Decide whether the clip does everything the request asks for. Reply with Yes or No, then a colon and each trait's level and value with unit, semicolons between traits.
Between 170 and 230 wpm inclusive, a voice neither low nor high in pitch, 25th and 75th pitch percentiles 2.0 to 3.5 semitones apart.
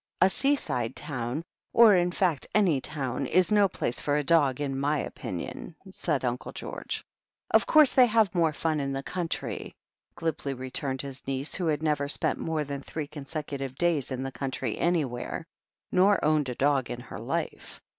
No: average, 175 wpm; medium, 150 Hz; average, 4.2 semitones